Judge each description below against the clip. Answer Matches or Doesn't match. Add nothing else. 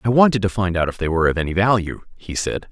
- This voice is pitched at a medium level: Doesn't match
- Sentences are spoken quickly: Matches